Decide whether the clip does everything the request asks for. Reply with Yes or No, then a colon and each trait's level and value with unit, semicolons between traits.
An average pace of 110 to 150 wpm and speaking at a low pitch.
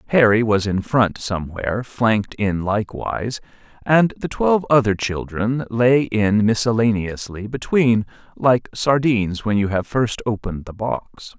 Yes: slow, 135 wpm; low, 110 Hz